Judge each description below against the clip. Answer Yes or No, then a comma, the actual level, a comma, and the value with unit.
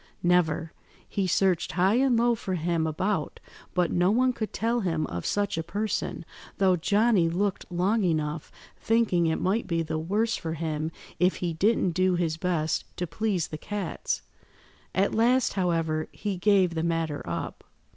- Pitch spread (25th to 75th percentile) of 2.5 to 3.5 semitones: No, average, 4.1 semitones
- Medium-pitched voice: Yes, medium, 180 Hz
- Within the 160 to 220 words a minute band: Yes, average, 165 wpm